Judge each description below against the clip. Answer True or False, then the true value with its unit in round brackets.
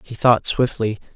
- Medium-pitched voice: False (115 Hz)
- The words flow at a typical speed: True (155 wpm)